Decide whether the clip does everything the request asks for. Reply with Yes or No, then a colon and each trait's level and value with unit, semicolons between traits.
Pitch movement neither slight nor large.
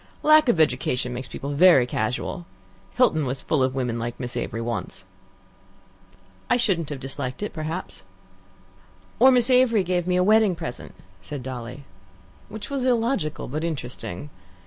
No: wide, 8.5 semitones